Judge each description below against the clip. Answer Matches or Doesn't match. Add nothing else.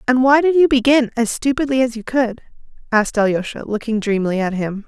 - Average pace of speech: Matches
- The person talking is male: Doesn't match